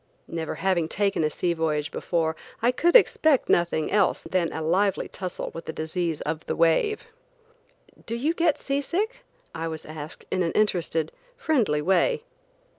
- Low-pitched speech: No, medium, 175 Hz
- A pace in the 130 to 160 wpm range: No, average, 170 wpm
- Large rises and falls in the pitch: Yes, wide, 7.5 semitones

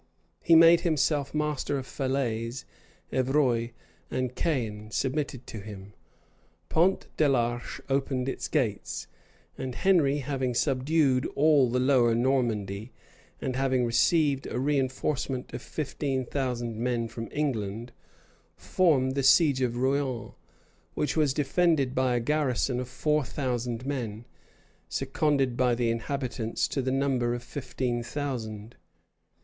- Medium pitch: No, low, 130 Hz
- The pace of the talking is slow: Yes, slow, 125 wpm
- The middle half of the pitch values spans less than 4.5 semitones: Yes, average, 2.9 semitones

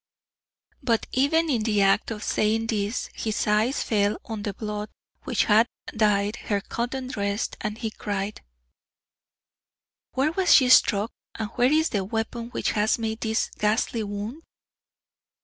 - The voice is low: No, high, 220 Hz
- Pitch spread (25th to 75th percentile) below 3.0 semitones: Yes, narrow, 2.4 semitones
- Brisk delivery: No, average, 150 wpm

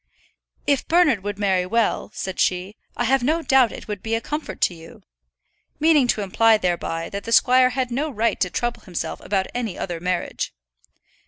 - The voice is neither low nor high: No, high, 225 Hz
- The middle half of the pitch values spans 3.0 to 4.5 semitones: No, average, 5.3 semitones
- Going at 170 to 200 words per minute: Yes, average, 185 wpm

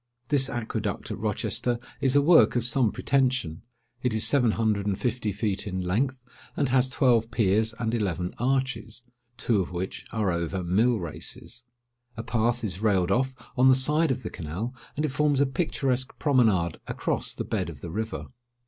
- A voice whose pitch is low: Yes, low, 115 Hz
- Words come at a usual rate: Yes, average, 180 wpm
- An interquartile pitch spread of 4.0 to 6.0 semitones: Yes, average, 4.5 semitones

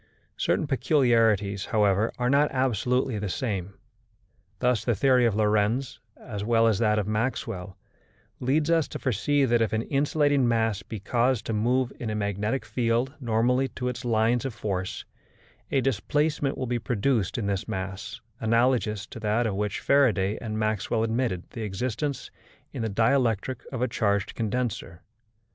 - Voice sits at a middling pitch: No, low, 115 Hz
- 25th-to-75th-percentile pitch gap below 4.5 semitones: Yes, average, 3.4 semitones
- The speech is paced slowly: No, average, 160 wpm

